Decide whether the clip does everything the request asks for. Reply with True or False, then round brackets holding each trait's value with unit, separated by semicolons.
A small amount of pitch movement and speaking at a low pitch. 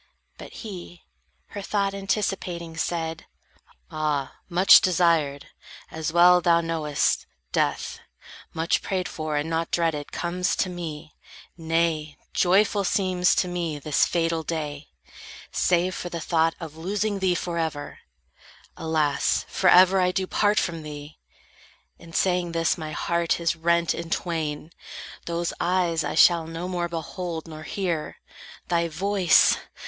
False (2.0 semitones; 170 Hz)